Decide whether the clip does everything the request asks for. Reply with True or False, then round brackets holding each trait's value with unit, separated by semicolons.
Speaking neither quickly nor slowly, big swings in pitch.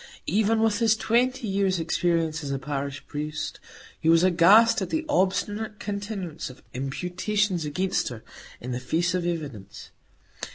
True (150 wpm; 5.8 semitones)